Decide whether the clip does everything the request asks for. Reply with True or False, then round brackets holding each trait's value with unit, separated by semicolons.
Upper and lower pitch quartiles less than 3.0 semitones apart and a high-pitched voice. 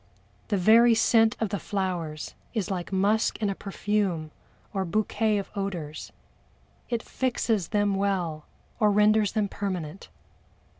True (2.6 semitones; 200 Hz)